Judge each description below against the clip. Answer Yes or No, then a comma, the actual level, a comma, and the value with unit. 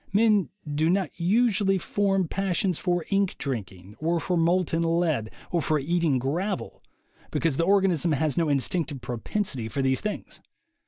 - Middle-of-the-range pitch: Yes, medium, 170 Hz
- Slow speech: No, average, 150 wpm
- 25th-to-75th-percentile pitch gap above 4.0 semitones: Yes, average, 4.9 semitones